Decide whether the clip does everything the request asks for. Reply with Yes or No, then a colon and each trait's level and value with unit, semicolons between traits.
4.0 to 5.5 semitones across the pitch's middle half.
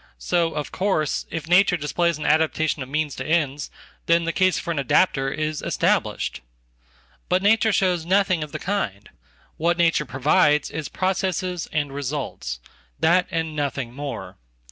No: average, 3.5 semitones